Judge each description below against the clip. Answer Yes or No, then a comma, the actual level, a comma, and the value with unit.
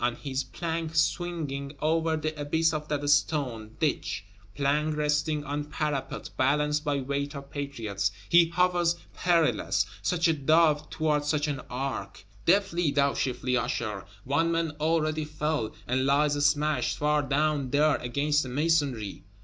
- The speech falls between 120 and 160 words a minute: Yes, average, 145 wpm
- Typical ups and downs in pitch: No, narrow, 2.3 semitones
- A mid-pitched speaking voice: Yes, medium, 150 Hz